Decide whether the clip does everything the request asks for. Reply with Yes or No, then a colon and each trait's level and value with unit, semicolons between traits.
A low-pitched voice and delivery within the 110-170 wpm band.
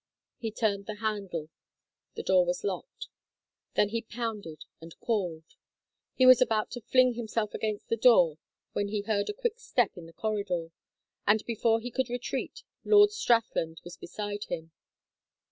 No: high, 220 Hz; average, 160 wpm